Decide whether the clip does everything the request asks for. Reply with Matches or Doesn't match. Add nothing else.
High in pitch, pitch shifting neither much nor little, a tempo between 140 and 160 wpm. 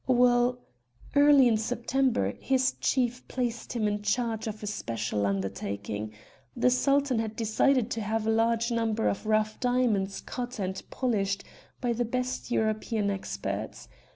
Matches